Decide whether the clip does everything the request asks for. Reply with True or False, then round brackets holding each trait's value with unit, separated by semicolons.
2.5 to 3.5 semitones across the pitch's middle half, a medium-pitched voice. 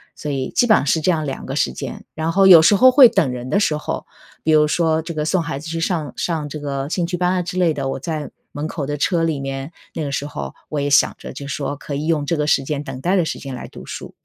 True (3.2 semitones; 155 Hz)